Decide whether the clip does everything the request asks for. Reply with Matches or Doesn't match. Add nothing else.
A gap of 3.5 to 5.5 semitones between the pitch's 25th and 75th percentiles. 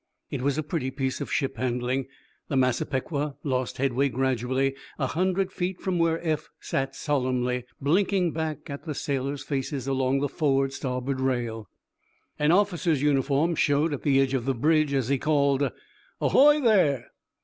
Doesn't match